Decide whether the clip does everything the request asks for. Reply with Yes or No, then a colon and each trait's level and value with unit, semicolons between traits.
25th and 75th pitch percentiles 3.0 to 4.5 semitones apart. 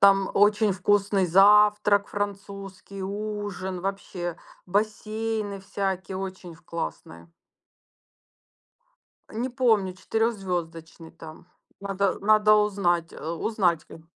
No: narrow, 2.4 semitones